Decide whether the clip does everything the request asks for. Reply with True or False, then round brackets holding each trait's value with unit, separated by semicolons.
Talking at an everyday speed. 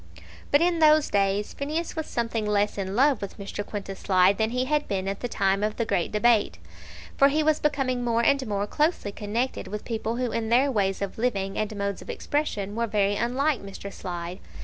False (210 wpm)